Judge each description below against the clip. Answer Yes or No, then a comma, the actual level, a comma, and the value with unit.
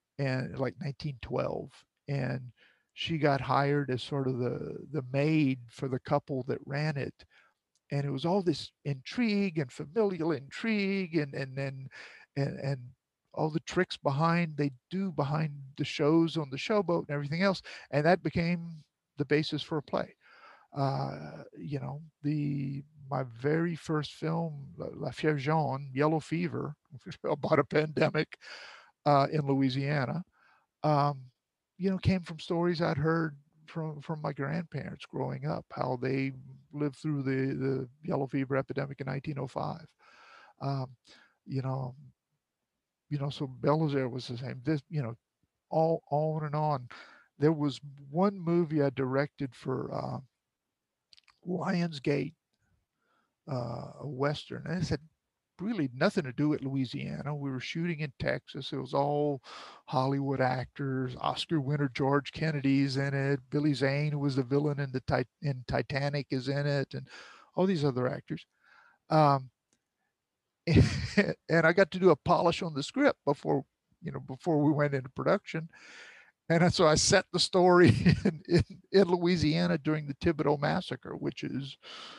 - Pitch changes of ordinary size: Yes, average, 3.1 semitones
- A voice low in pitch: No, medium, 145 Hz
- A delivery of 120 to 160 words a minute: Yes, average, 150 wpm